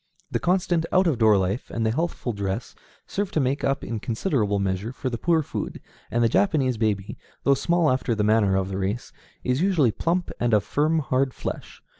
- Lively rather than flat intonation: Yes, wide, 6.8 semitones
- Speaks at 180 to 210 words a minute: Yes, fast, 205 wpm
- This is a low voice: Yes, low, 125 Hz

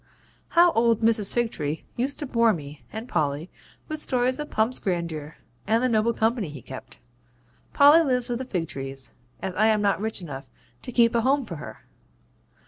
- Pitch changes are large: Yes, wide, 7.0 semitones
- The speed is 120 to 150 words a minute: No, average, 180 wpm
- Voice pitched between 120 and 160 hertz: No, high, 220 Hz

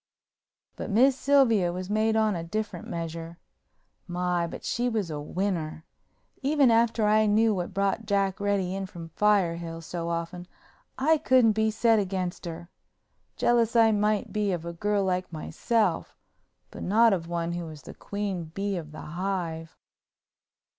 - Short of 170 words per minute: Yes, average, 160 wpm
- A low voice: No, high, 195 Hz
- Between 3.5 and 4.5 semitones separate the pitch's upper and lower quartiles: Yes, average, 4.2 semitones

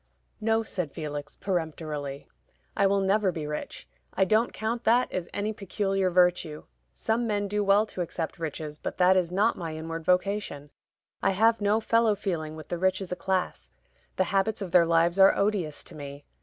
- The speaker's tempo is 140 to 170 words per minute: No, average, 185 wpm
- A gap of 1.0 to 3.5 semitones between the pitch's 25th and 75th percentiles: No, average, 4.0 semitones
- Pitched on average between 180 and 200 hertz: Yes, medium, 185 Hz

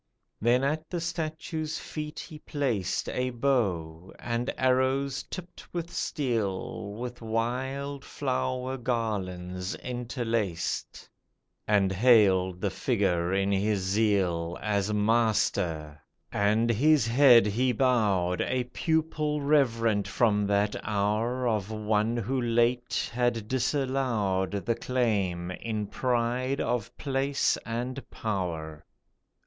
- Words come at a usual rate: No, slow, 110 wpm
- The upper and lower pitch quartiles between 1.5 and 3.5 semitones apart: No, average, 4.3 semitones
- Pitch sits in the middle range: No, low, 115 Hz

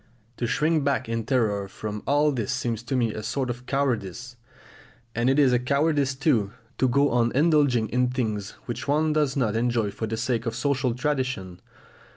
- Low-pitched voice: Yes, low, 125 Hz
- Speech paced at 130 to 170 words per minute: No, average, 190 wpm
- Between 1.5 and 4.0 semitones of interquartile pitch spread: Yes, average, 3.5 semitones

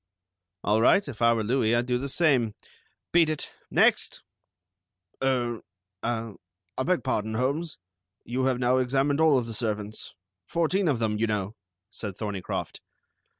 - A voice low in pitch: Yes, low, 120 Hz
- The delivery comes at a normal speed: Yes, average, 150 wpm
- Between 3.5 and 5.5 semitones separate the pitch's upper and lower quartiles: Yes, average, 4.1 semitones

